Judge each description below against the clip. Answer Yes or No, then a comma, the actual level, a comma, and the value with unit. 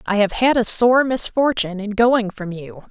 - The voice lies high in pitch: Yes, high, 220 Hz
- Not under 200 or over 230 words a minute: Yes, fast, 205 wpm